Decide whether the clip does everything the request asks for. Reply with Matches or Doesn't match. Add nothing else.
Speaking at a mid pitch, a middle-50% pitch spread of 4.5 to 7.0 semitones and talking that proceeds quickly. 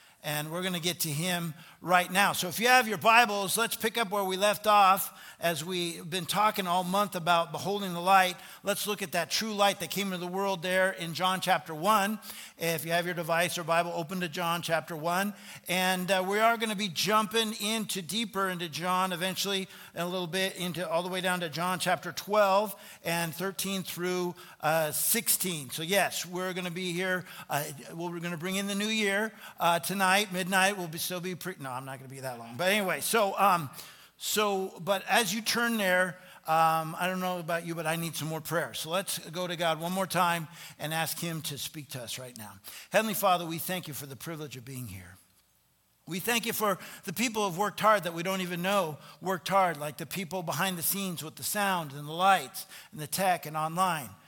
Doesn't match